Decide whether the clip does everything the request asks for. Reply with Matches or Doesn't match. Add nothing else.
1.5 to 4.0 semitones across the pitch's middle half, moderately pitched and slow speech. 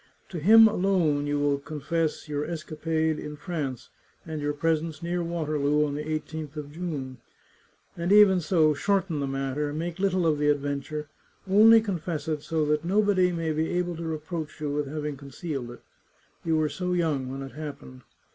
Doesn't match